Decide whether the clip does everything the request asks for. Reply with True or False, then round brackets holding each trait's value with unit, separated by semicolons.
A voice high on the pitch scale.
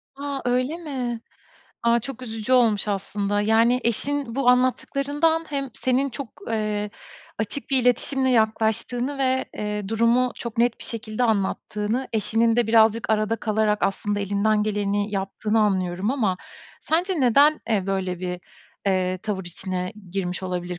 True (220 Hz)